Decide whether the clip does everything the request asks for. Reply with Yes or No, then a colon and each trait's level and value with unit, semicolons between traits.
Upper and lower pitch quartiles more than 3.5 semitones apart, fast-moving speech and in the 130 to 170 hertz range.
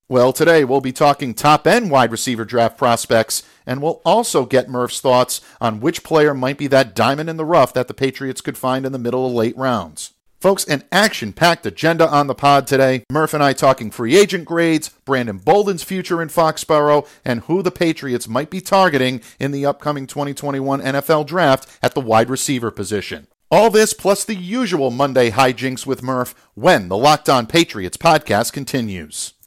No: average, 4.3 semitones; average, 185 wpm; low, 135 Hz